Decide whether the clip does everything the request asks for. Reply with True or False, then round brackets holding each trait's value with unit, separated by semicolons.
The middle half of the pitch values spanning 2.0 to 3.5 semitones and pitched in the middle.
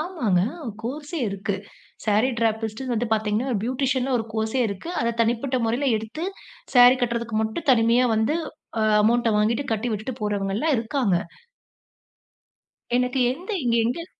False (2.9 semitones; 235 Hz)